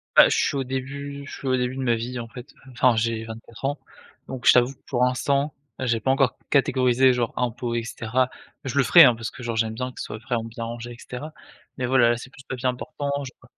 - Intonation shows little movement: Yes, narrow, 2.2 semitones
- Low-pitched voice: Yes, low, 125 Hz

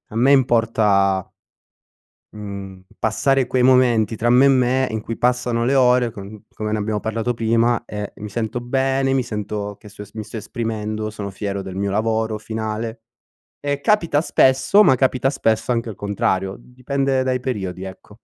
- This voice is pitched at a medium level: No, low, 115 Hz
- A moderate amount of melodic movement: Yes, average, 3.3 semitones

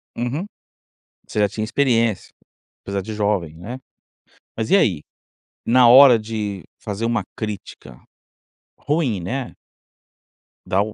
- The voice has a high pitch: No, low, 110 Hz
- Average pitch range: Yes, average, 3.5 semitones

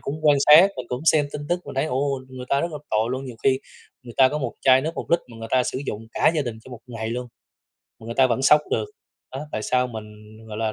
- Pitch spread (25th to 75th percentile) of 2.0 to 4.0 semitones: Yes, average, 3.7 semitones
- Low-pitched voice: Yes, low, 130 Hz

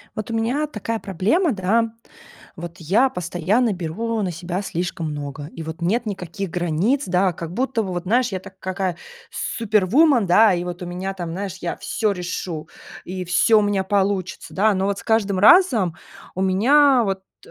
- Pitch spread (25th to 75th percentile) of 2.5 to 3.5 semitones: No, average, 4.1 semitones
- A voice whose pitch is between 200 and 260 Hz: No, high, 190 Hz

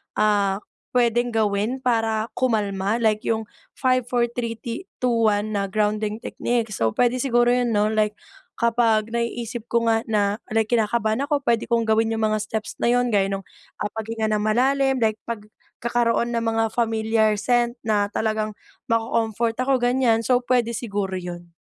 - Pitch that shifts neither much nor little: No, narrow, 2.0 semitones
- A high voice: Yes, high, 225 Hz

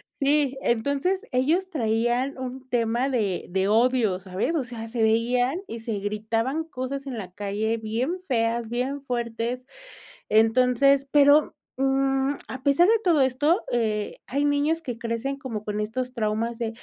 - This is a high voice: Yes, very high, 250 Hz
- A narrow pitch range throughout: No, average, 3.5 semitones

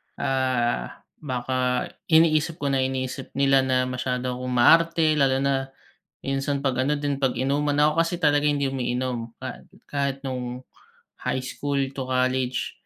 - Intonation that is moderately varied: No, narrow, 2.0 semitones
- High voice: No, low, 135 Hz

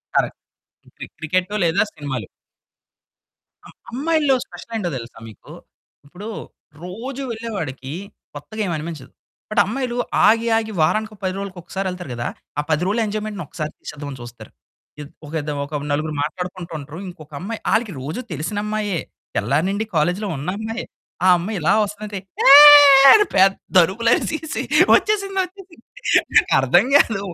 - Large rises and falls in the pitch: Yes, wide, 6.3 semitones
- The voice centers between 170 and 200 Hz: Yes, high, 190 Hz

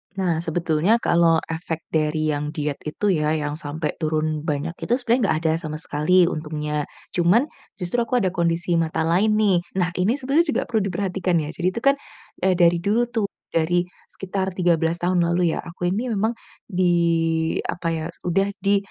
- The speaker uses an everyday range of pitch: Yes, average, 3.3 semitones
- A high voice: No, medium, 170 Hz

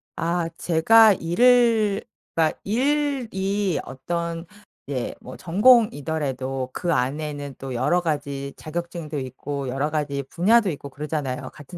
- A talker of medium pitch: Yes, medium, 160 Hz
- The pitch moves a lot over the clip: Yes, wide, 5.7 semitones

